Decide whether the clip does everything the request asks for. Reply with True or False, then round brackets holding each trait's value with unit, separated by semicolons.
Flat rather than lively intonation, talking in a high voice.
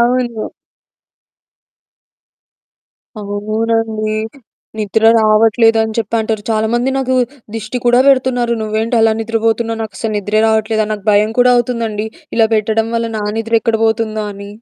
True (1.2 semitones; 225 Hz)